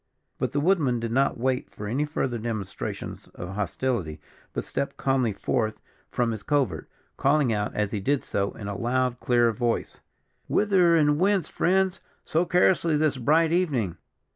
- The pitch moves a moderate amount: No, wide, 5.7 semitones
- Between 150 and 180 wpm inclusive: Yes, average, 165 wpm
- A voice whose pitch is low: Yes, low, 130 Hz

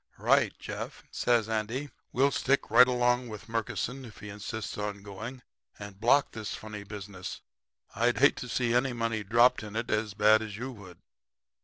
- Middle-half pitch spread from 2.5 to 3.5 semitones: Yes, average, 2.8 semitones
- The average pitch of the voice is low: Yes, low, 110 Hz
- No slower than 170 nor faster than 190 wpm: Yes, average, 175 wpm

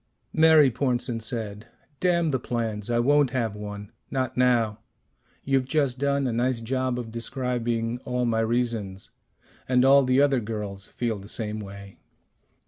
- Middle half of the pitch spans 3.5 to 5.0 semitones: No, average, 2.9 semitones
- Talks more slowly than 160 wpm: Yes, average, 150 wpm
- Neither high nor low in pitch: No, low, 120 Hz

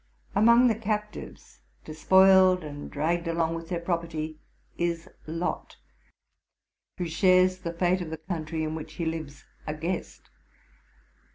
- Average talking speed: No, slow, 130 wpm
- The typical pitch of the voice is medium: Yes, medium, 170 Hz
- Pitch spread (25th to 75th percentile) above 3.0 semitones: No, narrow, 2.6 semitones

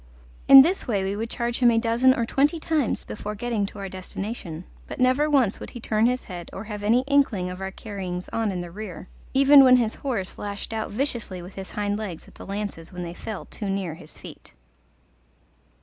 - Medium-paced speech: No, fast, 215 wpm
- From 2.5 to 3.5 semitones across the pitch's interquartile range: No, average, 4.3 semitones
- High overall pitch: Yes, high, 210 Hz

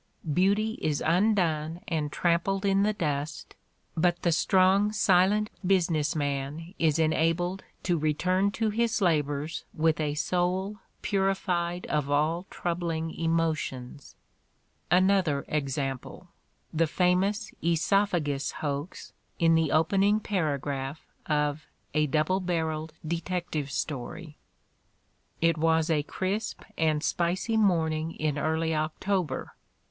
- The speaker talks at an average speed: No, slow, 110 wpm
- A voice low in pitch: No, medium, 165 Hz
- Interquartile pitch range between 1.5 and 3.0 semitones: No, average, 3.4 semitones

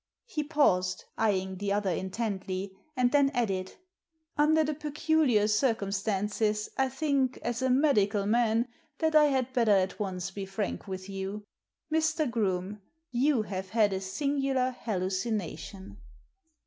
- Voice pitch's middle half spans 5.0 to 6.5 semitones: Yes, wide, 5.6 semitones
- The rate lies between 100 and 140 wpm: Yes, slow, 135 wpm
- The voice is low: No, high, 215 Hz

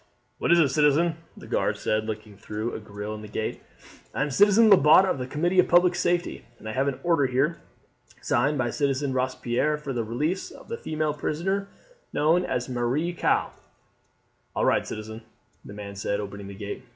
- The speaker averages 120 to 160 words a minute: No, average, 190 wpm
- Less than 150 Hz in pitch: Yes, low, 135 Hz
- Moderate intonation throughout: No, wide, 7.3 semitones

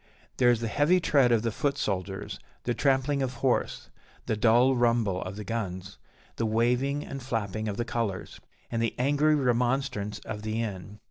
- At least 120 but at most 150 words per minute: No, average, 180 wpm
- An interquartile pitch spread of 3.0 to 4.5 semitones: Yes, average, 3.8 semitones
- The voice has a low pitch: Yes, low, 115 Hz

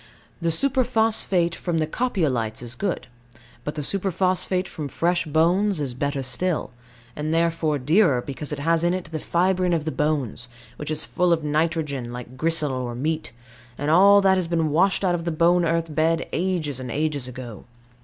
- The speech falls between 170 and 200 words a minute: Yes, average, 180 wpm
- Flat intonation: No, average, 3.7 semitones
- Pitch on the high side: No, medium, 160 Hz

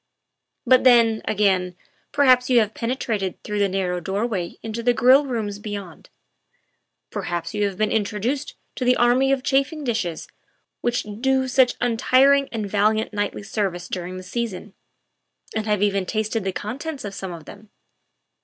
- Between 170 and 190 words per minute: No, average, 155 wpm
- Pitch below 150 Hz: No, high, 215 Hz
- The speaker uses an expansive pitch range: No, average, 4.0 semitones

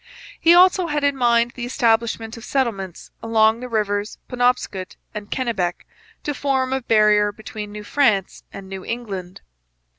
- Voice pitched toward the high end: Yes, high, 225 Hz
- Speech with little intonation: No, average, 3.5 semitones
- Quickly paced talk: No, average, 150 wpm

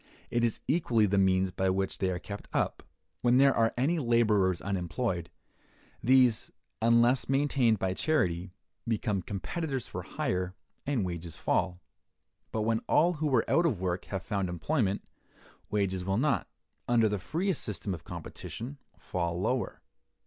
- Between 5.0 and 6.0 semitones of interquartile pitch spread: Yes, average, 5.3 semitones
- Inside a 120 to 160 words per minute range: Yes, average, 150 wpm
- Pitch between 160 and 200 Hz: No, low, 105 Hz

